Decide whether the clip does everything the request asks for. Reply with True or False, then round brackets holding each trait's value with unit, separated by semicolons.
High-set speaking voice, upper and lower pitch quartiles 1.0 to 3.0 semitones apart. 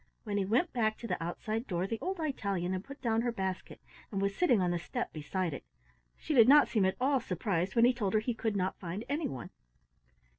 False (215 Hz; 4.5 semitones)